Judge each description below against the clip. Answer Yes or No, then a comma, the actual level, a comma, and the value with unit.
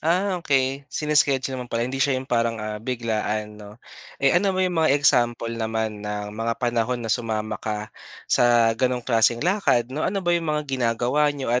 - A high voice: No, low, 120 Hz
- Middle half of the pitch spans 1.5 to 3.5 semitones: No, average, 4.3 semitones